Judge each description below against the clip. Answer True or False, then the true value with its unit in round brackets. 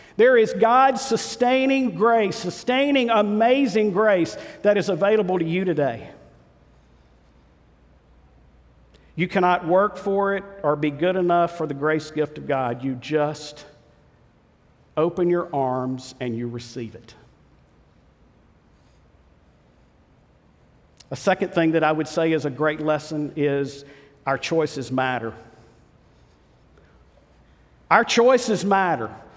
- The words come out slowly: True (115 wpm)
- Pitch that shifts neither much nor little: False (7.4 semitones)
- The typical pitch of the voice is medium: True (155 Hz)